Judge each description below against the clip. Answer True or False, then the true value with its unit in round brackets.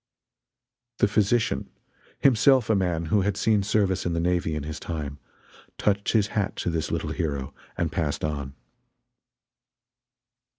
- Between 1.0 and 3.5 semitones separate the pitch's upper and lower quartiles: False (5.0 semitones)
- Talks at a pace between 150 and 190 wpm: False (140 wpm)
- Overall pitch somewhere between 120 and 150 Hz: False (90 Hz)